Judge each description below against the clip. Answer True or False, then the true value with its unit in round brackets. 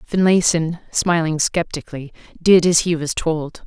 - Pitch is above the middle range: False (165 Hz)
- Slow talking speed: True (130 wpm)